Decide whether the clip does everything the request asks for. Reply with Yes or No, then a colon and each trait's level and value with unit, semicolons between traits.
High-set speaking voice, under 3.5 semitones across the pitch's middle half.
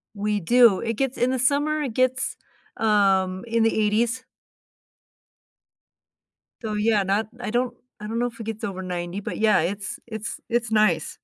Yes: high, 220 Hz; average, 2.9 semitones